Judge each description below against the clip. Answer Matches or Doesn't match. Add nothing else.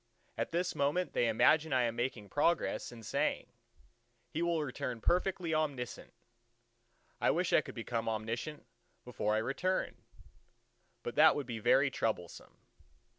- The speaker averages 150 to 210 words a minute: Doesn't match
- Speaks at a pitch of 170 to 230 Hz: Doesn't match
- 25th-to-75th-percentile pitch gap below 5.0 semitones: Doesn't match